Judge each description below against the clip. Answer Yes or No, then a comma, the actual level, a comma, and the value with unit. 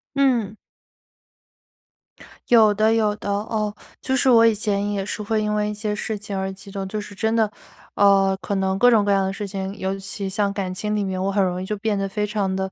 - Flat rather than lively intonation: Yes, narrow, 1.7 semitones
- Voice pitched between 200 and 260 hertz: Yes, high, 205 Hz